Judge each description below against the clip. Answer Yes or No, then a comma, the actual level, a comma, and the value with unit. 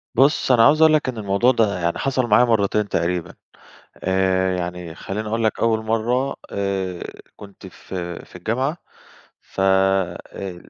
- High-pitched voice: No, low, 100 Hz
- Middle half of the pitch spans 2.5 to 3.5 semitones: No, average, 4.1 semitones